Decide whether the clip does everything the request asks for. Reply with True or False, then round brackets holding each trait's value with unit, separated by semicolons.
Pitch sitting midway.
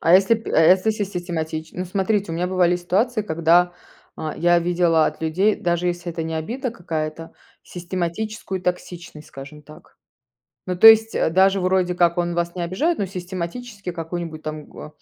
True (175 Hz)